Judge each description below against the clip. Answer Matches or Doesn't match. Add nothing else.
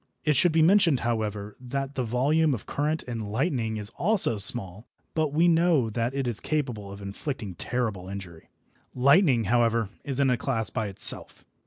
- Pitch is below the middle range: Matches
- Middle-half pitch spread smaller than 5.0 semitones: Doesn't match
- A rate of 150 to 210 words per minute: Matches